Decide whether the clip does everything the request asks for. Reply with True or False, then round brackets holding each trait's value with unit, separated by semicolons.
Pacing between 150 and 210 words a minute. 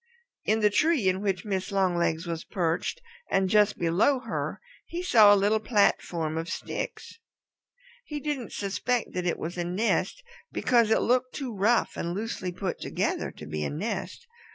True (170 wpm)